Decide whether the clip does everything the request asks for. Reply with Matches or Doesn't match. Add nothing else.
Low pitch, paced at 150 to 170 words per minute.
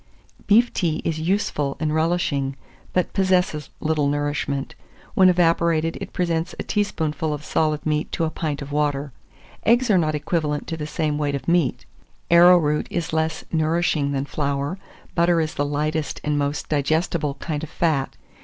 Doesn't match